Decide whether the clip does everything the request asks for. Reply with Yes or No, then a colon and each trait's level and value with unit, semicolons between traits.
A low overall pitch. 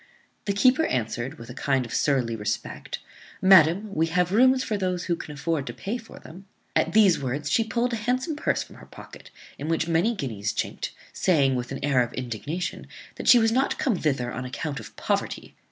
No: medium, 165 Hz